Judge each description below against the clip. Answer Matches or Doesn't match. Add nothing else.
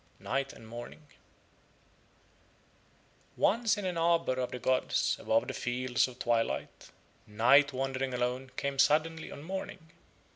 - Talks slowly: Matches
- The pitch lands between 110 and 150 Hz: Matches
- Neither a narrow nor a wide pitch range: Matches